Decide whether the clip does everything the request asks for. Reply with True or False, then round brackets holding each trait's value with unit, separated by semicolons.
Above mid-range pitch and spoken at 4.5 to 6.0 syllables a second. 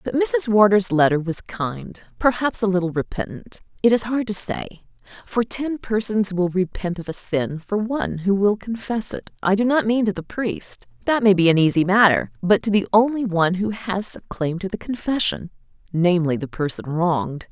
True (200 Hz; 5.0 syllables/s)